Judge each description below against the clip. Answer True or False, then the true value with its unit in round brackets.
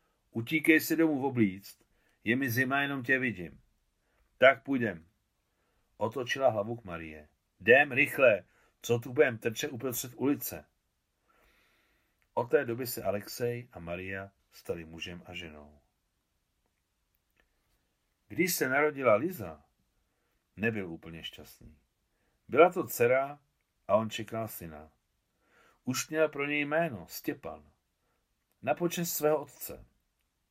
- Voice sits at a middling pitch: False (120 Hz)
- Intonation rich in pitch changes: True (7.9 semitones)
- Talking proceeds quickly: False (120 wpm)